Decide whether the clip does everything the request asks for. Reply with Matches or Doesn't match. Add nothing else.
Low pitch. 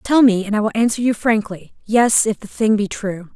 Doesn't match